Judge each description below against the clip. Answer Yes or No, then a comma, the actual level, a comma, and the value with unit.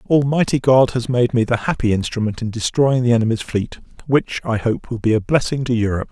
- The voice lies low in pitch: Yes, low, 120 Hz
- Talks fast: Yes, fast, 215 wpm